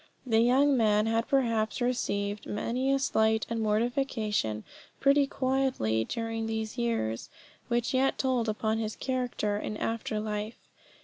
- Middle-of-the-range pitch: No, high, 225 Hz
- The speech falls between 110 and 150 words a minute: Yes, slow, 135 wpm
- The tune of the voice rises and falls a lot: No, average, 3.2 semitones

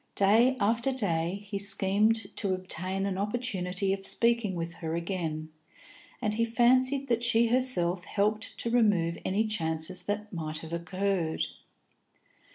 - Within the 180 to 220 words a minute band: No, average, 140 wpm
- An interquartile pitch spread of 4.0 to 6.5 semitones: Yes, average, 4.4 semitones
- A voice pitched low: No, high, 200 Hz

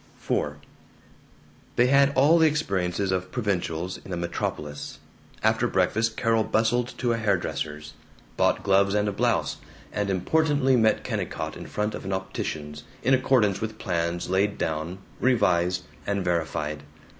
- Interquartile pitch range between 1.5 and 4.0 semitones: No, average, 4.9 semitones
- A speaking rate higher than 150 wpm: No, average, 145 wpm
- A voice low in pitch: Yes, low, 100 Hz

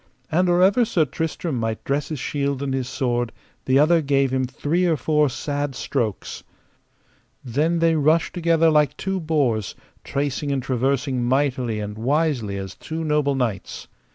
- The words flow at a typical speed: Yes, average, 160 wpm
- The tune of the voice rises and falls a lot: No, average, 3.9 semitones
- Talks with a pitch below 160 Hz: Yes, medium, 140 Hz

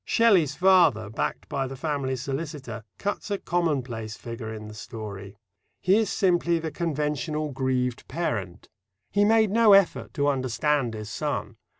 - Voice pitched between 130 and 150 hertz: Yes, medium, 140 Hz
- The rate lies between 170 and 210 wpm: No, average, 150 wpm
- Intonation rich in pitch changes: Yes, wide, 6.8 semitones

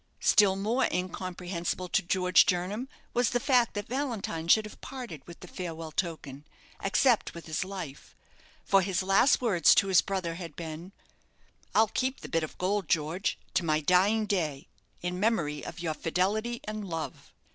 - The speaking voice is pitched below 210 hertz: Yes, medium, 185 Hz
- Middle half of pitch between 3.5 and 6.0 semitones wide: Yes, average, 4.2 semitones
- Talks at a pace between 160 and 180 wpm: Yes, average, 170 wpm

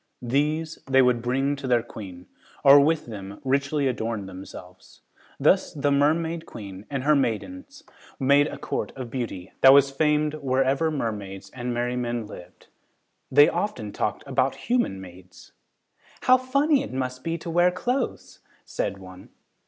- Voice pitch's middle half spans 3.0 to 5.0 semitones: No, wide, 5.6 semitones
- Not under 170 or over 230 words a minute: No, average, 150 wpm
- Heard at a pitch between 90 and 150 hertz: Yes, low, 135 Hz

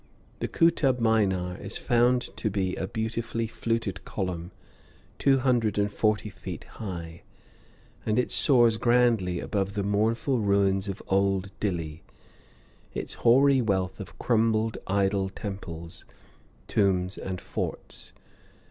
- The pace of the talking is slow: Yes, slow, 120 wpm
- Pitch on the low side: Yes, low, 105 Hz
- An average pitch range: Yes, average, 3.2 semitones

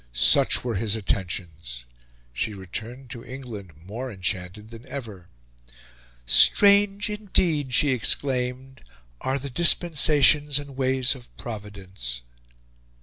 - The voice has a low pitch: Yes, low, 125 Hz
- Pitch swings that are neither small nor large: No, wide, 5.9 semitones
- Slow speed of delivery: Yes, slow, 105 wpm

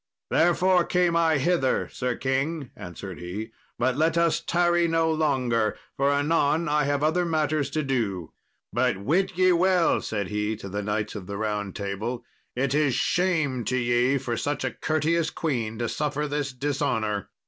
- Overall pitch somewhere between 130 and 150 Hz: Yes, medium, 140 Hz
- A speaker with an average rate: Yes, average, 170 wpm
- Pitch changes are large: Yes, wide, 6.1 semitones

